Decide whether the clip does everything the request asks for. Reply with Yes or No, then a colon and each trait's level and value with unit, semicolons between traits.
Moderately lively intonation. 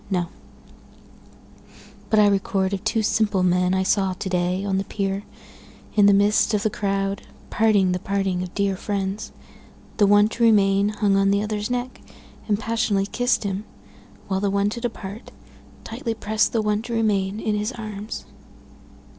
No: narrow, 1.8 semitones